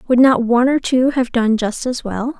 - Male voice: No, female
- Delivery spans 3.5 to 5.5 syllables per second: Yes, 5.0 syllables/s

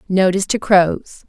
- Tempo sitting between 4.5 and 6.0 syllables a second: Yes, 4.6 syllables/s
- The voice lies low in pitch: No, high, 190 Hz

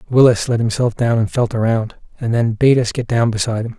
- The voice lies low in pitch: Yes, low, 115 Hz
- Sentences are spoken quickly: Yes, fast, 240 wpm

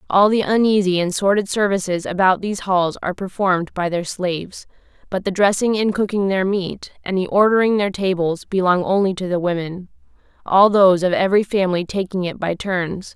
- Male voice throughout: No, female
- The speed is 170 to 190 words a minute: Yes, average, 180 wpm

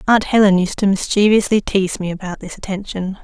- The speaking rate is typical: Yes, average, 185 wpm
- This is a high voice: Yes, high, 195 Hz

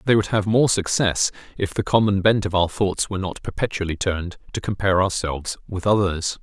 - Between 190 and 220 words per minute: Yes, average, 195 wpm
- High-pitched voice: No, very low, 95 Hz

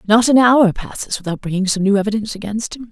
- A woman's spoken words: Yes, female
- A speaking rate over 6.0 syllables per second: Yes, 6.6 syllables/s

